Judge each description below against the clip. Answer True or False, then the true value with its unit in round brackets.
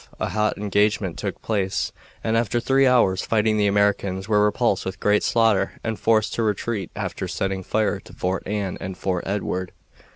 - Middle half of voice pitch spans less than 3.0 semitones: True (2.5 semitones)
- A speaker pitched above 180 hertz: False (105 Hz)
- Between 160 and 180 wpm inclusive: True (175 wpm)